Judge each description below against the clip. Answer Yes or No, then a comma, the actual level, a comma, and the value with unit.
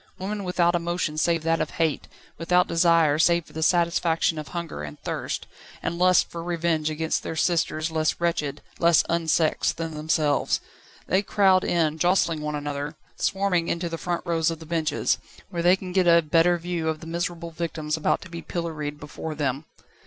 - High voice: No, medium, 165 Hz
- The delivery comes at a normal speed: Yes, average, 180 wpm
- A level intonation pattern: Yes, narrow, 1.8 semitones